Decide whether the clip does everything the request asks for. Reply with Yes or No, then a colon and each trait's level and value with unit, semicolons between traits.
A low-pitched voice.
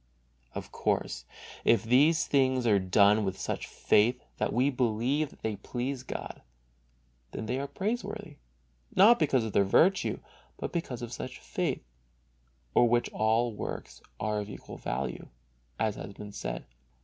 Yes: low, 120 Hz